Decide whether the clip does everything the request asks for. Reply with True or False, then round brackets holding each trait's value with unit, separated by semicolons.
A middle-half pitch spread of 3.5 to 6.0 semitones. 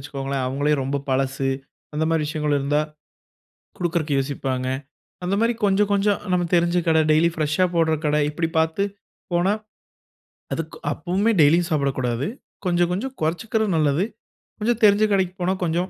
True (4.1 semitones)